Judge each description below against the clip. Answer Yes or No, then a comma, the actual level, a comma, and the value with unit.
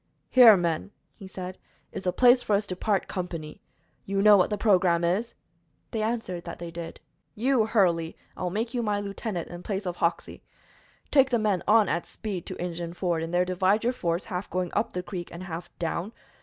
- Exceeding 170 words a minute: Yes, fast, 205 wpm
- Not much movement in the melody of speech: No, average, 3.6 semitones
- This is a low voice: No, medium, 185 Hz